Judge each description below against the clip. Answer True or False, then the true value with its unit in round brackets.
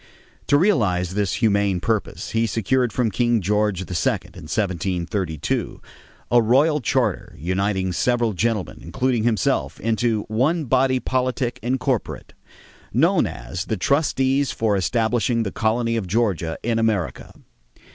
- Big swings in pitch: False (4.3 semitones)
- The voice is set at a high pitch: False (110 Hz)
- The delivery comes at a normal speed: False (130 wpm)